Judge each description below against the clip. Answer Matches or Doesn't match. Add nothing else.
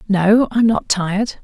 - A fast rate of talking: Doesn't match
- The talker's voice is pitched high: Matches